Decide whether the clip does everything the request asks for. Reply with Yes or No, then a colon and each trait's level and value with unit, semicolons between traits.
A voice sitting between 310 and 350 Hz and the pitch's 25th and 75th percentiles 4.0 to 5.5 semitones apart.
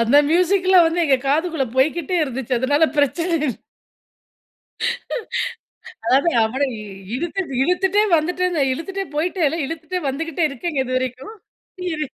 Yes: very high, 320 Hz; average, 4.9 semitones